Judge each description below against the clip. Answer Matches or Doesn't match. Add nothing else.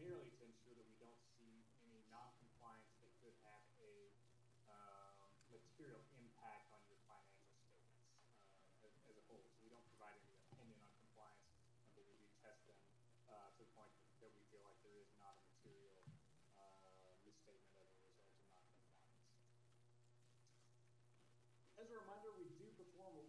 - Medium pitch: Doesn't match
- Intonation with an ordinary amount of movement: Doesn't match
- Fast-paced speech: Doesn't match